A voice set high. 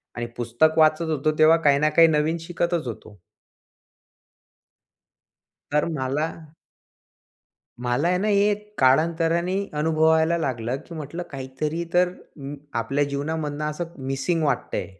No: medium, 155 Hz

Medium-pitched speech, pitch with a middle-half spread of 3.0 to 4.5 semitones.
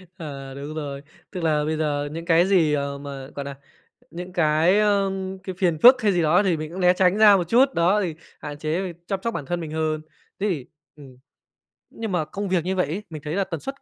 Yes: medium, 170 Hz; average, 4.0 semitones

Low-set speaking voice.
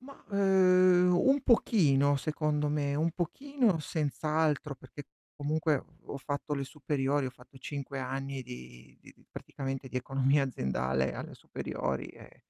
No: medium, 145 Hz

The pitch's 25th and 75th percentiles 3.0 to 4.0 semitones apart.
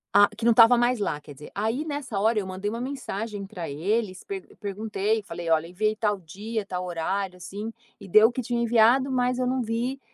Yes: average, 3.6 semitones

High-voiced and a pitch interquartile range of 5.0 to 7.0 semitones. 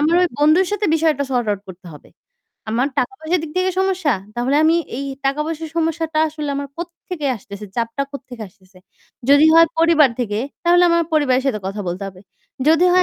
Yes: very high, 295 Hz; wide, 5.4 semitones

